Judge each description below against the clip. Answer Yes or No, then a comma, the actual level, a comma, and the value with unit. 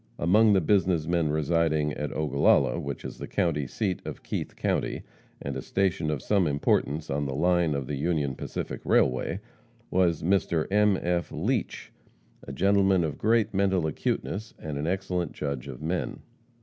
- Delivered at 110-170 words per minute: Yes, average, 165 wpm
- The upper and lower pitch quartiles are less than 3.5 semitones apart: No, average, 4.3 semitones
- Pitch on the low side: Yes, very low, 85 Hz